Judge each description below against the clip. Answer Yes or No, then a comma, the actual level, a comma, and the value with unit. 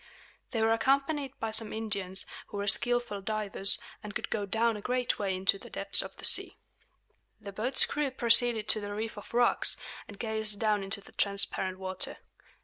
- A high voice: Yes, high, 215 Hz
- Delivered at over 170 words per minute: Yes, average, 185 wpm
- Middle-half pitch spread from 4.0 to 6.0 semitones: No, average, 2.7 semitones